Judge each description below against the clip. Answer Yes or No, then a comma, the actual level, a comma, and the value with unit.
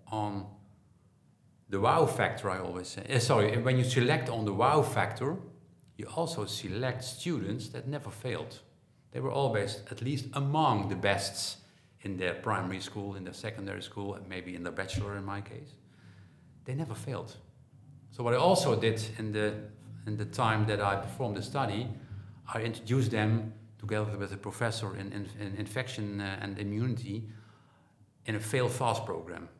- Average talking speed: Yes, average, 165 wpm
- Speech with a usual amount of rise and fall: Yes, average, 4.0 semitones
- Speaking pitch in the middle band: No, low, 110 Hz